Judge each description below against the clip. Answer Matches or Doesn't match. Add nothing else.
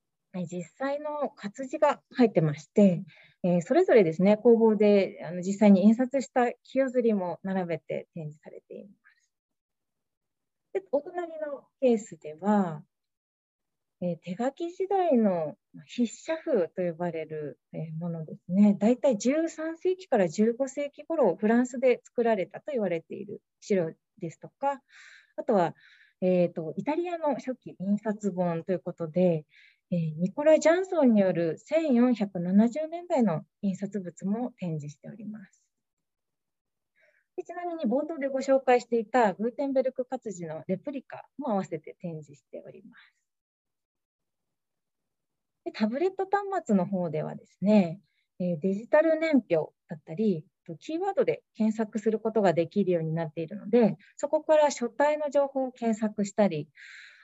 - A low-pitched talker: Doesn't match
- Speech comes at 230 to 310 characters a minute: Matches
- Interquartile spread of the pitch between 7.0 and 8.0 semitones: Matches